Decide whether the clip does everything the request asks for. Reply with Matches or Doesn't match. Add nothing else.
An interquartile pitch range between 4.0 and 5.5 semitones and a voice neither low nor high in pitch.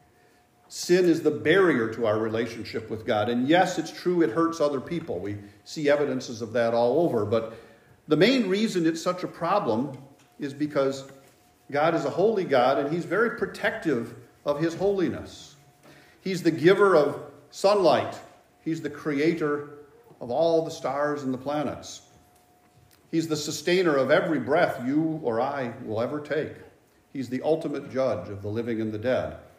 Matches